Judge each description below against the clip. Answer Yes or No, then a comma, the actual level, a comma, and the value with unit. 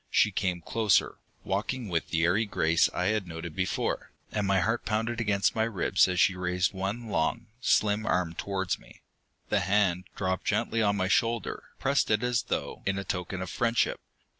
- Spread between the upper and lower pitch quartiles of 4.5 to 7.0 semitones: No, average, 3.4 semitones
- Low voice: Yes, low, 100 Hz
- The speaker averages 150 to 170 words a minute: No, average, 180 wpm